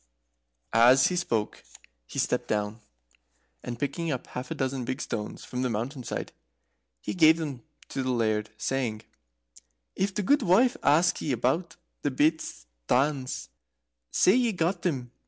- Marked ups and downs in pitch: Yes, wide, 5.7 semitones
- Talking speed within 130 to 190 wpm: Yes, average, 160 wpm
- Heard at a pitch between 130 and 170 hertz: Yes, low, 135 Hz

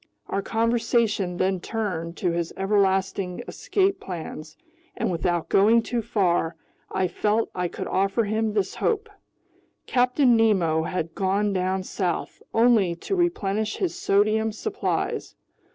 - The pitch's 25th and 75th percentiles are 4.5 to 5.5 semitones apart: No, average, 3.8 semitones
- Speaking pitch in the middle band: No, high, 200 Hz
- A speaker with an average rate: No, slow, 130 wpm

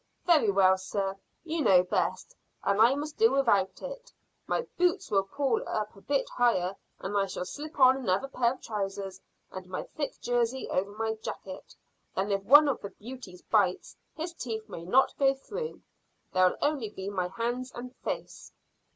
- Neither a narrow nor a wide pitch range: No, wide, 5.8 semitones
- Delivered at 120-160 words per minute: No, average, 175 wpm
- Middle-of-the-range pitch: No, high, 225 Hz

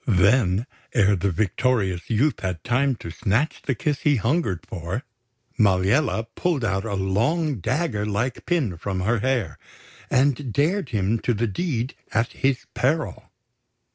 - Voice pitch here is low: Yes, low, 115 Hz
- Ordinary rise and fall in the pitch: No, wide, 5.8 semitones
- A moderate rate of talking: Yes, average, 145 wpm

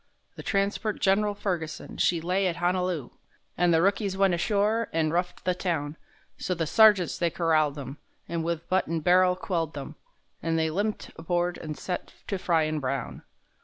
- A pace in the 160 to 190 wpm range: Yes, average, 170 wpm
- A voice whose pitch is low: No, medium, 175 Hz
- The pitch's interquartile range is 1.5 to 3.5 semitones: Yes, average, 2.9 semitones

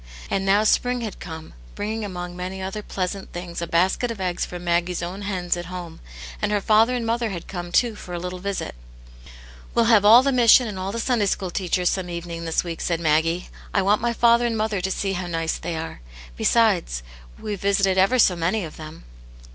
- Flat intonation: No, average, 3.6 semitones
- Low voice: No, high, 190 Hz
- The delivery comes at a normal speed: No, fast, 220 wpm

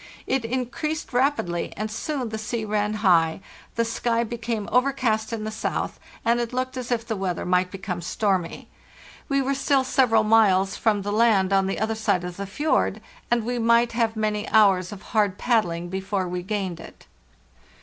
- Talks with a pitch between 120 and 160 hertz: No, high, 220 Hz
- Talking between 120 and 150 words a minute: No, average, 180 wpm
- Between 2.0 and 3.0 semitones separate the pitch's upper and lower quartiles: No, average, 3.5 semitones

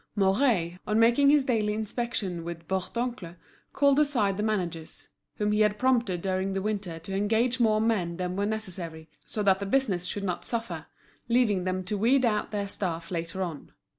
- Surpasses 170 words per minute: Yes, average, 180 wpm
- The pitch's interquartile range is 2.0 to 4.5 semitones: Yes, average, 4.0 semitones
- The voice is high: Yes, high, 205 Hz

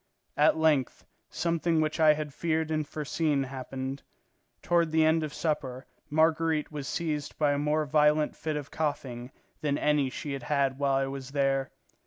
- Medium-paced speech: Yes, average, 170 wpm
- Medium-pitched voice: Yes, medium, 150 Hz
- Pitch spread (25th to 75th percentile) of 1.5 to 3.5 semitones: Yes, narrow, 2.4 semitones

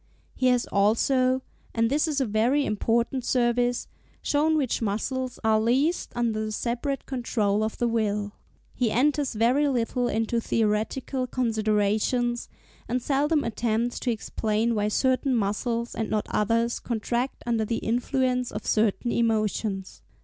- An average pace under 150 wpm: Yes, average, 140 wpm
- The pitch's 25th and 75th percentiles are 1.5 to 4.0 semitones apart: Yes, average, 2.8 semitones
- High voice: Yes, high, 235 Hz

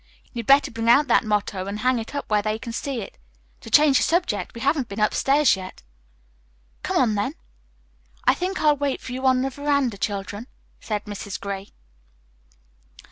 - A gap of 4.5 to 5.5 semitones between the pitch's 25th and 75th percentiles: Yes, average, 5.1 semitones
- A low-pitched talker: No, high, 235 Hz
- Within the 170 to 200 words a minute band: Yes, average, 185 wpm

